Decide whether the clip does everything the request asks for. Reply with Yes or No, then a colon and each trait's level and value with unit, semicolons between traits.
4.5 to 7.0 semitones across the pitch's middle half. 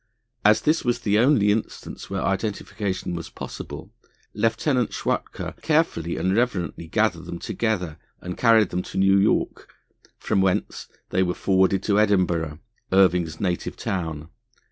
No: average, 3.5 semitones